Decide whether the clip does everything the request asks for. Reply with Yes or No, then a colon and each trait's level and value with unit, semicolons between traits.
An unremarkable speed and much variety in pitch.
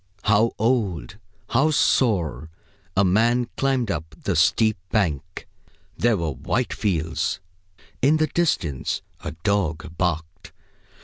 No: slow, 115 wpm; wide, 6.5 semitones